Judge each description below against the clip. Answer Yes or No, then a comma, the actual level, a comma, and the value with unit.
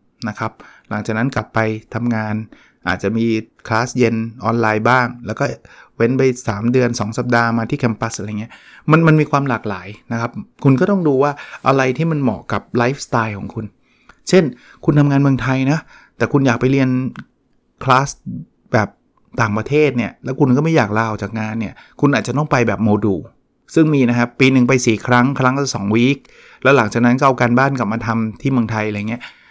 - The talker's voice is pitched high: No, low, 120 Hz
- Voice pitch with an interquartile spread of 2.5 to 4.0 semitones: Yes, average, 3.3 semitones